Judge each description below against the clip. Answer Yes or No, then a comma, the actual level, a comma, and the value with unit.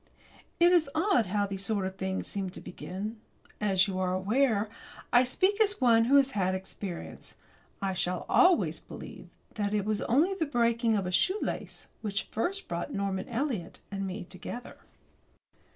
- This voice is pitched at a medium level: No, high, 210 Hz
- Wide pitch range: Yes, wide, 6.0 semitones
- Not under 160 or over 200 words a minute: Yes, average, 170 wpm